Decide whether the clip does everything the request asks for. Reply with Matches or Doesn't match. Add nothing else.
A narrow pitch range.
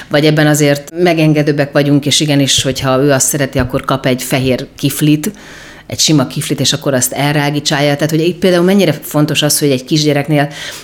Matches